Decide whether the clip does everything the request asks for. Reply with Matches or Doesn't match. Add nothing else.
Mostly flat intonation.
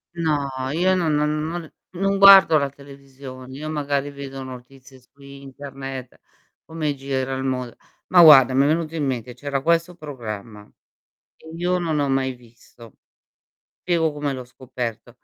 Doesn't match